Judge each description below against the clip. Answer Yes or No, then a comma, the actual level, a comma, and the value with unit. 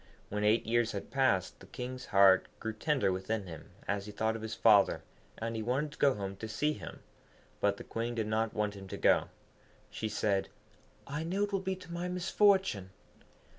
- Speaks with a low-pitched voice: Yes, low, 110 Hz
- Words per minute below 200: No, fast, 205 wpm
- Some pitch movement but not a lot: No, wide, 5.7 semitones